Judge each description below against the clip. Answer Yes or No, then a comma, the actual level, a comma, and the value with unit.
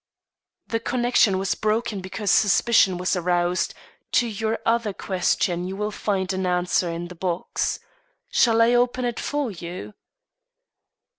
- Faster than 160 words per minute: No, average, 140 wpm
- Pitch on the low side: No, high, 195 Hz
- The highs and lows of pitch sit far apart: No, average, 4.2 semitones